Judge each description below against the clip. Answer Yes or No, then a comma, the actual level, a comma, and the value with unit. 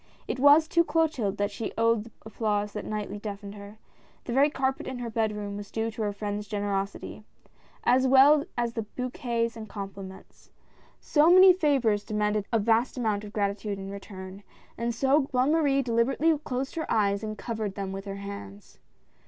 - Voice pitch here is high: Yes, high, 220 Hz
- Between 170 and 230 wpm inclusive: Yes, average, 185 wpm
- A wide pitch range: No, average, 4.3 semitones